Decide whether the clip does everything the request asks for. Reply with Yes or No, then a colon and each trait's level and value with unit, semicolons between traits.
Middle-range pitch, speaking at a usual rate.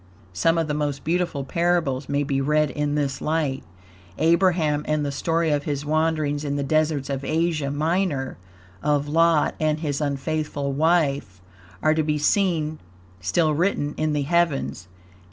Yes: medium, 150 Hz; average, 155 wpm